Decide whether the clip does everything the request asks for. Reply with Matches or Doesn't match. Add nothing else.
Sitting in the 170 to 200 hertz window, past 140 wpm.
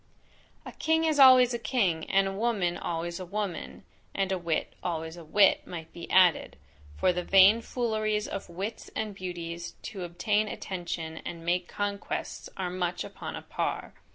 Matches